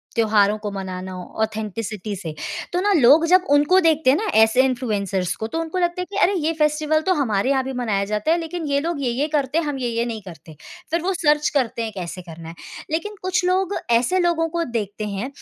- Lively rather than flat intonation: Yes, wide, 7.5 semitones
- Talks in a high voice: Yes, very high, 265 Hz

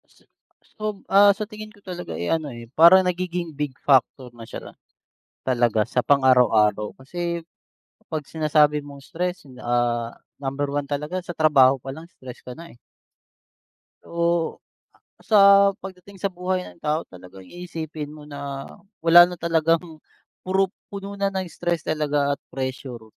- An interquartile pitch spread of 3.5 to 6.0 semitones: Yes, average, 4.8 semitones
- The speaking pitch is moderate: Yes, medium, 155 Hz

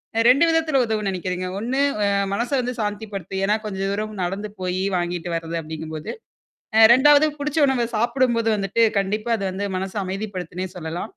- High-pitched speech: Yes, high, 205 Hz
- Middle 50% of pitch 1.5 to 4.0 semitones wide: No, average, 4.4 semitones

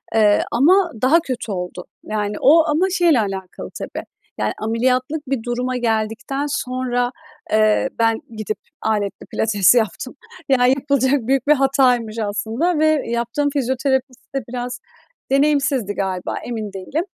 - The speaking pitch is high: Yes, very high, 250 Hz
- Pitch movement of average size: Yes, average, 4.0 semitones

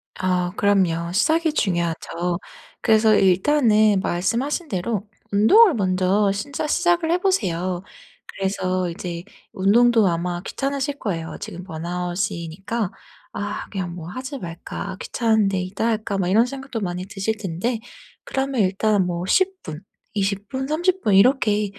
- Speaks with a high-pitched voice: Yes, high, 200 Hz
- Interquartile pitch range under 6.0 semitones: Yes, average, 5.1 semitones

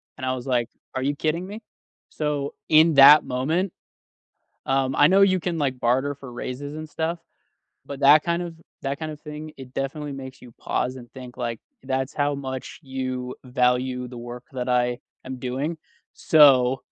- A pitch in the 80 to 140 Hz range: Yes, low, 135 Hz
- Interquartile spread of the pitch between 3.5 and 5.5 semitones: No, average, 3.1 semitones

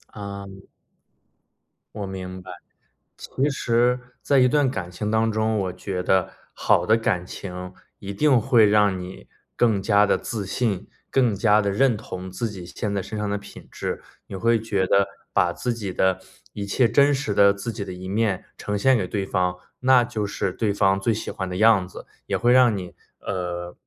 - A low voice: Yes, low, 100 Hz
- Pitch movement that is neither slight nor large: Yes, average, 3.3 semitones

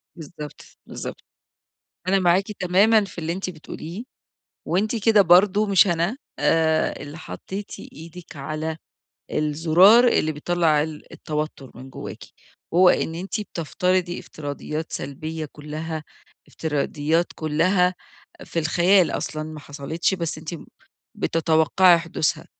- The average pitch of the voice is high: No, medium, 165 Hz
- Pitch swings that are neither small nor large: Yes, average, 3.1 semitones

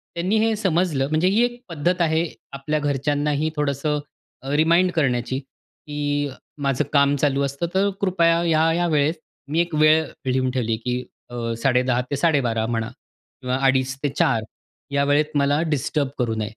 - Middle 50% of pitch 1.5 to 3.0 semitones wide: No, average, 3.6 semitones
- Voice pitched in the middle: Yes, medium, 145 Hz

